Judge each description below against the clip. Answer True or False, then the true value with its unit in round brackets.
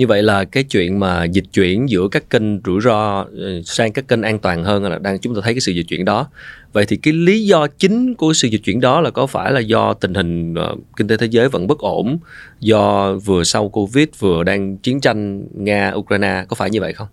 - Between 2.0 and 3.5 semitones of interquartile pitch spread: False (4.2 semitones)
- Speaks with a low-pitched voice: True (105 Hz)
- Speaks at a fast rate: False (240 wpm)